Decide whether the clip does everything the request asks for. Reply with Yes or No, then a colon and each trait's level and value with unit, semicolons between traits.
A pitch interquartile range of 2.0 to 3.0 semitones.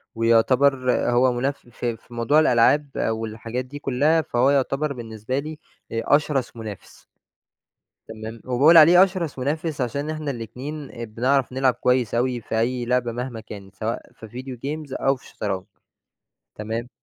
No: average, 3.6 semitones